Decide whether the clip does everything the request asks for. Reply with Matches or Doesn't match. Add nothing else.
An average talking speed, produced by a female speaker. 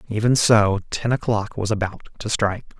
Doesn't match